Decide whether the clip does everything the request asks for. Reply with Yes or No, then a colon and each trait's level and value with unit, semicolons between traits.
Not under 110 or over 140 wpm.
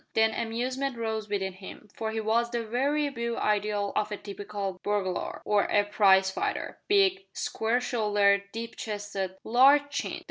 No: average, 155 wpm